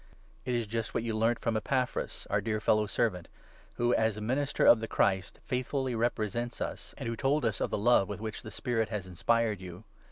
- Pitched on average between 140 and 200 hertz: No, low, 115 Hz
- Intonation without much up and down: Yes, narrow, 2.2 semitones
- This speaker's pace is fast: Yes, fast, 225 wpm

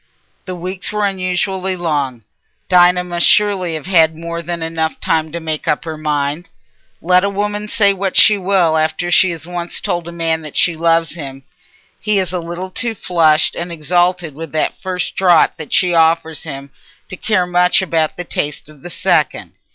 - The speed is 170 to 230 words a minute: Yes, average, 185 wpm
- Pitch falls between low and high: Yes, medium, 170 Hz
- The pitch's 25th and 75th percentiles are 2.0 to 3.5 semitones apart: Yes, narrow, 2.4 semitones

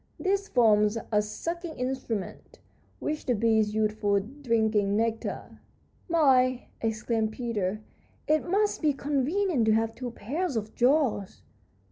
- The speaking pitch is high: Yes, high, 230 Hz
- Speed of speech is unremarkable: No, slow, 125 wpm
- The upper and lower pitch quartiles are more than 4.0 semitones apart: Yes, average, 5.3 semitones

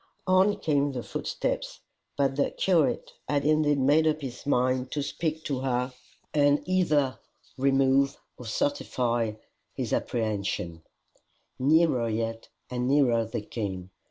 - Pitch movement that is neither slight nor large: Yes, average, 3.8 semitones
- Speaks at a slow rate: Yes, slow, 130 wpm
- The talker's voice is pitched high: No, low, 135 Hz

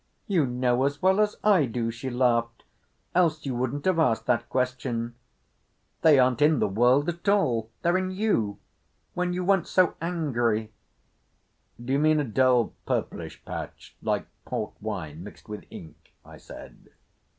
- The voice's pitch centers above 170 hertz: No, low, 130 Hz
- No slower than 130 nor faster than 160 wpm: Yes, average, 150 wpm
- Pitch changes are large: Yes, wide, 6.3 semitones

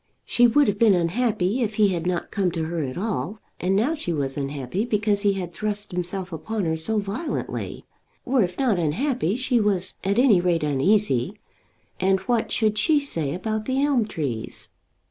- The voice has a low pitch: No, high, 200 Hz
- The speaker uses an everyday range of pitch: Yes, average, 4.6 semitones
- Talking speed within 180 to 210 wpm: Yes, average, 185 wpm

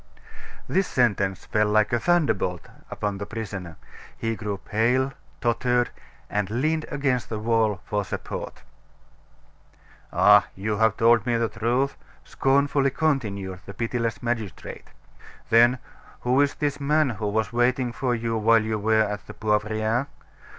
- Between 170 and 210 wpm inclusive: No, average, 140 wpm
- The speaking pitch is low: Yes, low, 115 Hz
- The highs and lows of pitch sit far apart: No, average, 3.1 semitones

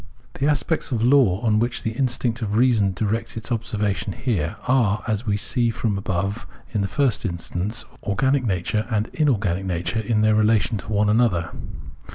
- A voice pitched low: Yes, low, 110 Hz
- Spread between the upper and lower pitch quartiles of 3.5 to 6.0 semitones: No, average, 3.1 semitones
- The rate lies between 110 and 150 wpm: No, average, 185 wpm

